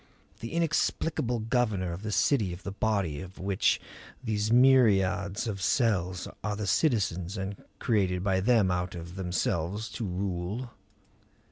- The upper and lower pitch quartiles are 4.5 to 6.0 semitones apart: No, average, 3.6 semitones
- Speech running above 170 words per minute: No, average, 140 wpm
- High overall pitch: No, low, 100 Hz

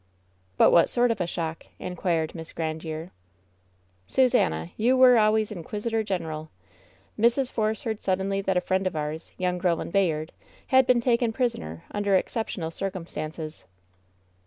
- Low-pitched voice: No, medium, 185 Hz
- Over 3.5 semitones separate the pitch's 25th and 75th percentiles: Yes, wide, 5.4 semitones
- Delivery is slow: No, average, 150 wpm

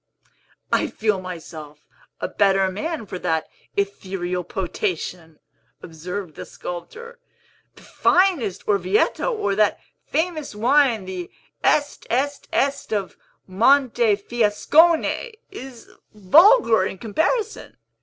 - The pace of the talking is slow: Yes, slow, 100 wpm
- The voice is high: Yes, high, 210 Hz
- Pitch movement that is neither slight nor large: No, wide, 7.5 semitones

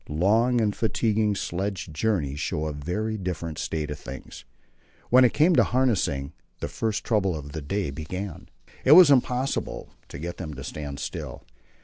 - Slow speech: No, average, 165 wpm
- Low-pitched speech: Yes, very low, 95 Hz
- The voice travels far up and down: Yes, wide, 6.6 semitones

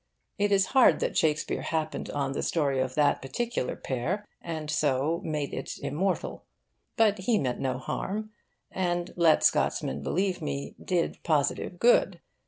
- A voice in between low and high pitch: Yes, medium, 160 Hz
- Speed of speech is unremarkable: Yes, average, 150 wpm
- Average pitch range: No, wide, 5.7 semitones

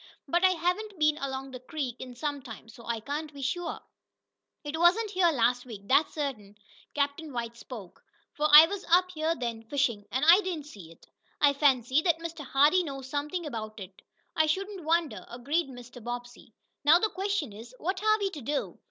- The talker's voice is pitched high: Yes, very high, 290 Hz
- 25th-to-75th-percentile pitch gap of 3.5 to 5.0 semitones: No, wide, 5.5 semitones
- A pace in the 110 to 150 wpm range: No, average, 195 wpm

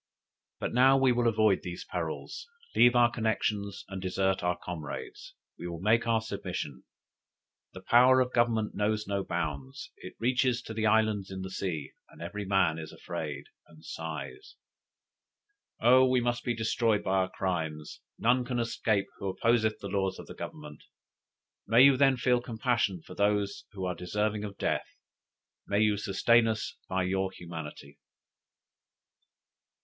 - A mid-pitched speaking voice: No, low, 105 Hz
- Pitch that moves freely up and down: No, average, 4.2 semitones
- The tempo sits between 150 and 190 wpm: Yes, average, 155 wpm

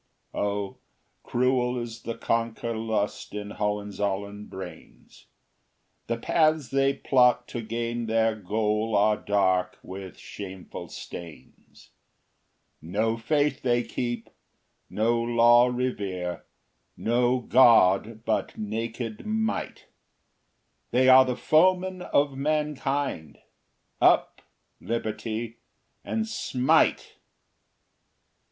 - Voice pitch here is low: Yes, low, 115 Hz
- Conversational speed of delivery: No, slow, 95 wpm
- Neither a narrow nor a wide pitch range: Yes, average, 3.6 semitones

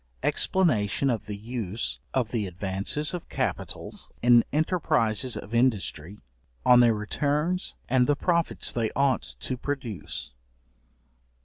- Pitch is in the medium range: No, low, 120 Hz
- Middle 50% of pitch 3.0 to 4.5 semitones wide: No, average, 5.3 semitones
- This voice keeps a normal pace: No, slow, 120 wpm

